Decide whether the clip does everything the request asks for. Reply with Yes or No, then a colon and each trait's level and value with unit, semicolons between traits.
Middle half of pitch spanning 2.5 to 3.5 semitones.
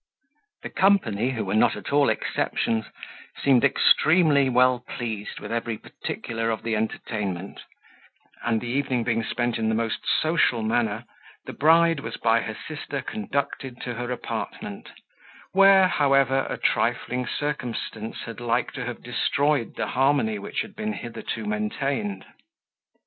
No: average, 4.3 semitones